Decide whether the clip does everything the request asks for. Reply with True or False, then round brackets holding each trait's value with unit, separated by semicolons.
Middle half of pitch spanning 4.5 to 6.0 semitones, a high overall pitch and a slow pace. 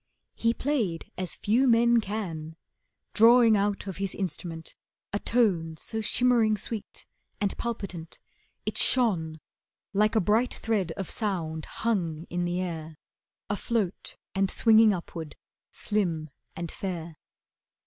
True (4.9 semitones; 195 Hz; 125 wpm)